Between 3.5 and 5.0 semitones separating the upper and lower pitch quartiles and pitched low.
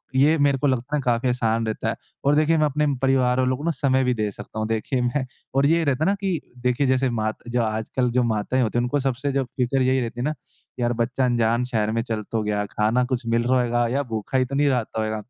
No: average, 2.7 semitones; low, 125 Hz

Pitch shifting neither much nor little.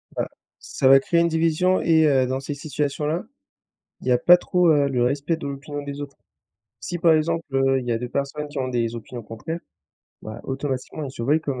Yes: average, 3.6 semitones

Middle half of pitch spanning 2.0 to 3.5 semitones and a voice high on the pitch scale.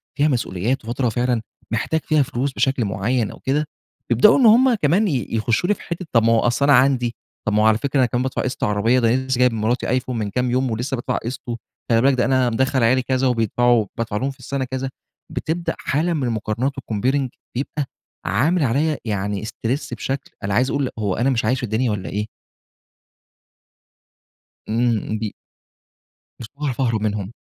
No: average, 3.2 semitones; low, 125 Hz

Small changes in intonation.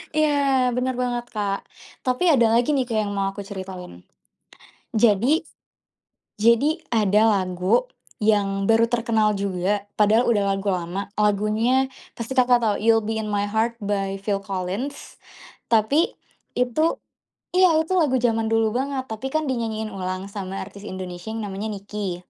No: average, 3.9 semitones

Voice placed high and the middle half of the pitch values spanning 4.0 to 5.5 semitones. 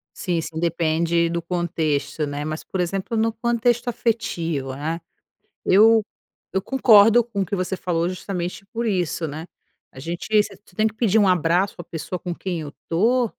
No: medium, 180 Hz; average, 4.8 semitones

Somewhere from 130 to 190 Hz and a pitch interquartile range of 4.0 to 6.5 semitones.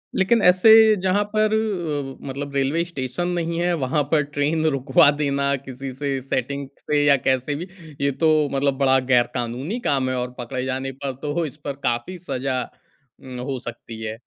No: medium, 140 Hz; average, 3.4 semitones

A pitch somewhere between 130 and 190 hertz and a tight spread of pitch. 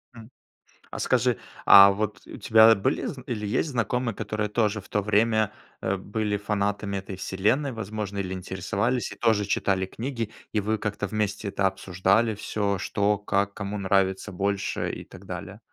No: low, 105 Hz; narrow, 2.0 semitones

